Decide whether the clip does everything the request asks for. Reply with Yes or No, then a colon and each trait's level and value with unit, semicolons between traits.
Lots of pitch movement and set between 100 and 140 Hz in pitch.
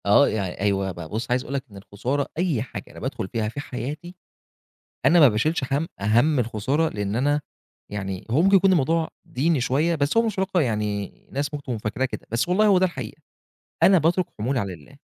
Yes: wide, 7.2 semitones; low, 135 Hz